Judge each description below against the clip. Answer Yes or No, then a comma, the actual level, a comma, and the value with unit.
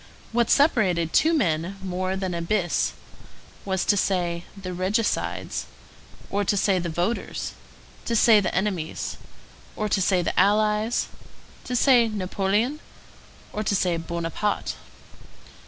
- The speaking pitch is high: Yes, high, 195 Hz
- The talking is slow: Yes, slow, 130 wpm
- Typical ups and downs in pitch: Yes, average, 3.2 semitones